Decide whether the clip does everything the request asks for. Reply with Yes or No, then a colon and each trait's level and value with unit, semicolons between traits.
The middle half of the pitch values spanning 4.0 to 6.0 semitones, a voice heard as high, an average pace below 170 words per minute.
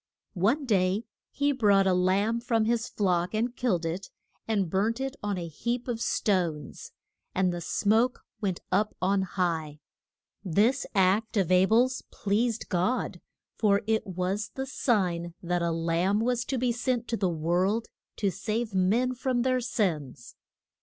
Yes: average, 4.5 semitones; high, 205 Hz; average, 160 wpm